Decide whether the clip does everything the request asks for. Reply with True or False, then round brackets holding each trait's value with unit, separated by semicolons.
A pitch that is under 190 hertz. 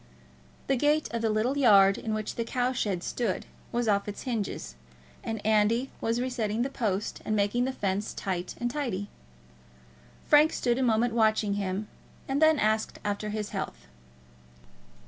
False (220 Hz)